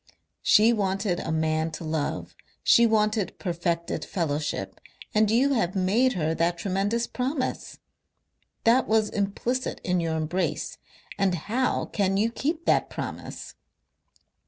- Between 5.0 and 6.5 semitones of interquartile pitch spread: Yes, average, 5.3 semitones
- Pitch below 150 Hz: No, high, 195 Hz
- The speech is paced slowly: Yes, slow, 130 wpm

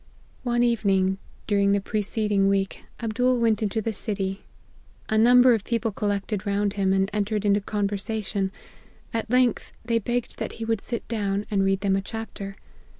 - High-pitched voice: Yes, high, 210 Hz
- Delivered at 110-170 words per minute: No, average, 180 wpm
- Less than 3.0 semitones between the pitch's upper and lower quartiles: Yes, narrow, 2.4 semitones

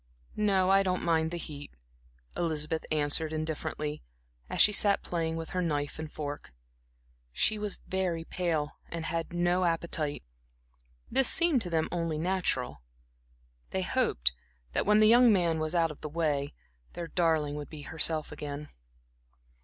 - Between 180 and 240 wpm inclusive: No, average, 155 wpm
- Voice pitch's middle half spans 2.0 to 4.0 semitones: Yes, average, 3.0 semitones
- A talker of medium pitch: Yes, medium, 165 Hz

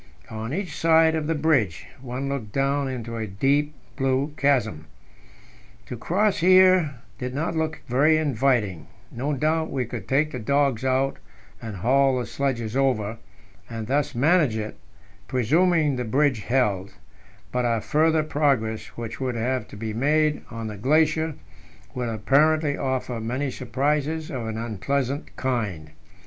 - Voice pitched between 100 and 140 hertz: Yes, low, 135 Hz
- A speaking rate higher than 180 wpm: No, average, 150 wpm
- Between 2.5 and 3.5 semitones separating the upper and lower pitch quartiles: No, average, 4.6 semitones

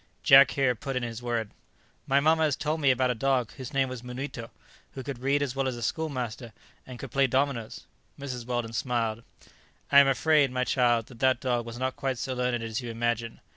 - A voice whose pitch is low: Yes, low, 125 Hz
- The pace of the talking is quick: Yes, fast, 215 wpm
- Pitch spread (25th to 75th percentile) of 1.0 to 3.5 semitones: Yes, narrow, 2.4 semitones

